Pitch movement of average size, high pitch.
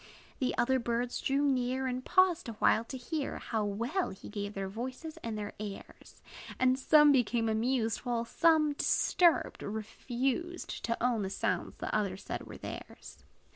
Yes: average, 3.9 semitones; high, 245 Hz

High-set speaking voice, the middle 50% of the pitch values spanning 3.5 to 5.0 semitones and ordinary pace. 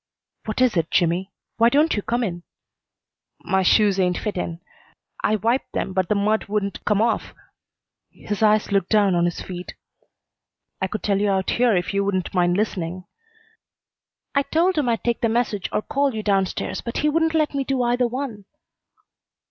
Yes: high, 210 Hz; average, 4.2 semitones; average, 185 wpm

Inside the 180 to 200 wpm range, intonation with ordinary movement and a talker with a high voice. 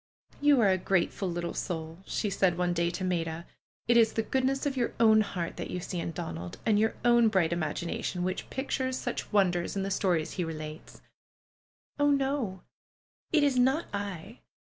No: average, 190 wpm; wide, 5.7 semitones; high, 195 Hz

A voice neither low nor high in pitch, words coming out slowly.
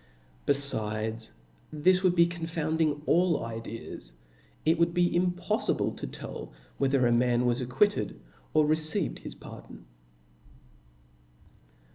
Yes: medium, 150 Hz; slow, 120 wpm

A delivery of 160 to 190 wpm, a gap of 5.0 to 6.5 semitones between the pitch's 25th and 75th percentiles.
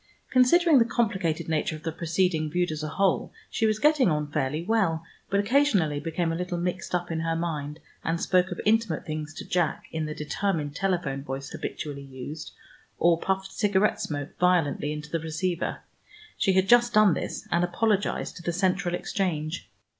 No: average, 180 wpm; average, 3.9 semitones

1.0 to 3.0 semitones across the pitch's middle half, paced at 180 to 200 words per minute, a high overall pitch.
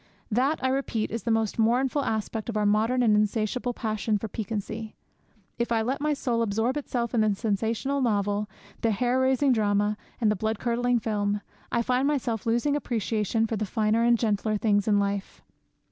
Yes: narrow, 2.6 semitones; average, 185 wpm; high, 225 Hz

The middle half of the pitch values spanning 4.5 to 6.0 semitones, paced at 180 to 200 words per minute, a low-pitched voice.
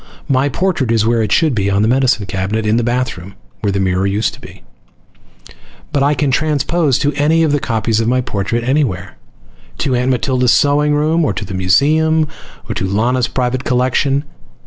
Yes: average, 5.1 semitones; average, 190 wpm; low, 125 Hz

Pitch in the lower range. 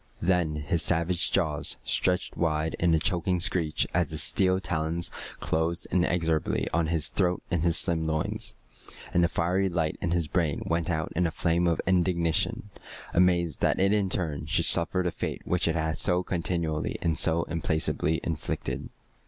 Yes: very low, 85 Hz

